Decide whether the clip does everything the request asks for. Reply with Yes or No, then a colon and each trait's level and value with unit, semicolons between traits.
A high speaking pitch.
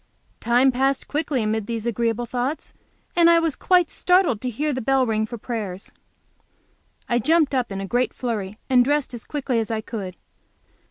Yes: high, 245 Hz